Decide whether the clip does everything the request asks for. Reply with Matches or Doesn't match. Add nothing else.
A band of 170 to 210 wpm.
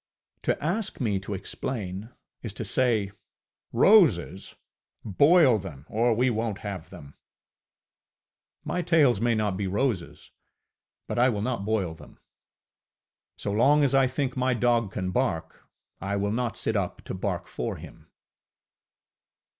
Doesn't match